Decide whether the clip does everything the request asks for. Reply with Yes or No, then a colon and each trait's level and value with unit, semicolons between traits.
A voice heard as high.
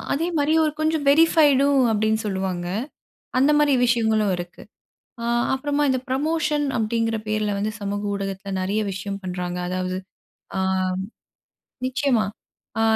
Yes: high, 220 Hz